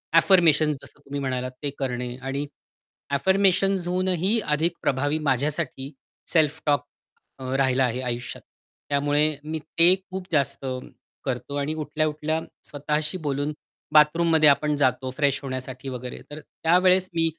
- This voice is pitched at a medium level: Yes, medium, 150 Hz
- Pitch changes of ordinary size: Yes, average, 3.4 semitones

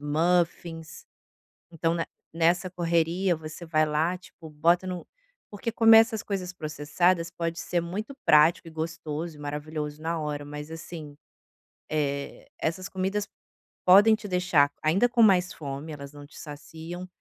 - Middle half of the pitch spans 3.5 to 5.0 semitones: No, average, 2.9 semitones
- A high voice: No, medium, 165 Hz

